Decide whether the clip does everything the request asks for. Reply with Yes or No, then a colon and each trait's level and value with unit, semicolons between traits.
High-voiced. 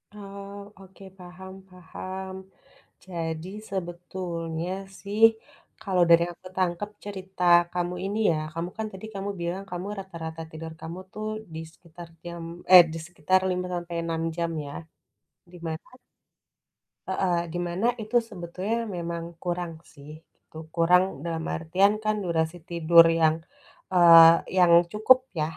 No: medium, 175 Hz